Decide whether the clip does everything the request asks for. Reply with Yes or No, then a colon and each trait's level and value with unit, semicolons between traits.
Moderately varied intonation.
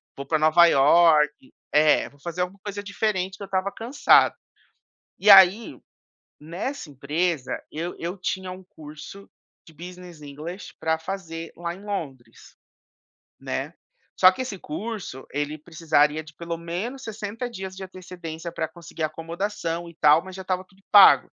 Yes: average, 3.5 semitones